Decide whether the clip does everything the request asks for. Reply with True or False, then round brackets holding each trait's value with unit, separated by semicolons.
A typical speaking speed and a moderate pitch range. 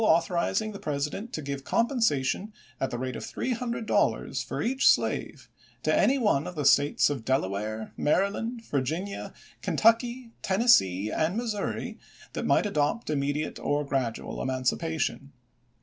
False (145 wpm; 8.5 semitones)